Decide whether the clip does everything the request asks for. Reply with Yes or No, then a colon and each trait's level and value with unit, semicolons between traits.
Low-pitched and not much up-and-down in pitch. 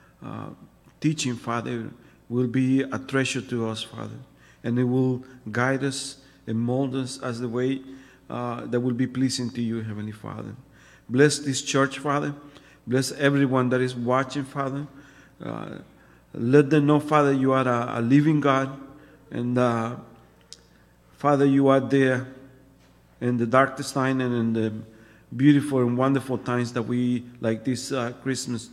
Yes: low, 130 Hz; narrow, 2.2 semitones